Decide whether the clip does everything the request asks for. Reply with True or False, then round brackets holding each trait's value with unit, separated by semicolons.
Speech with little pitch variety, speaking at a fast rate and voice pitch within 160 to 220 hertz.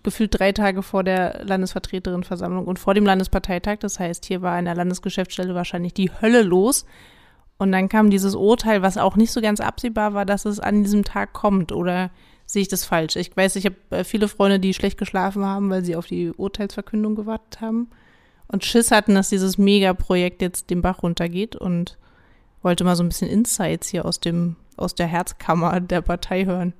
True (2.3 semitones; 195 wpm; 190 Hz)